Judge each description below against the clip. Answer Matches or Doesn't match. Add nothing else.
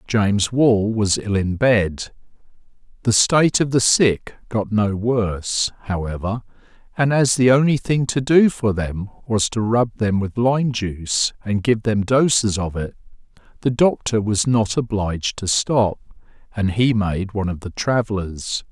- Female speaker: Doesn't match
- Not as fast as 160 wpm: Doesn't match